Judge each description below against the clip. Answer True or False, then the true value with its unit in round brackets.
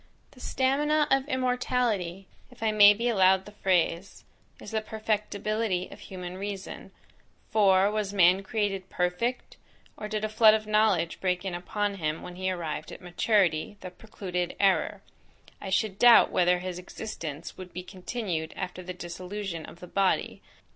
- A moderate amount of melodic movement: True (3.1 semitones)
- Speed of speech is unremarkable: True (160 wpm)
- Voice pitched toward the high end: True (195 Hz)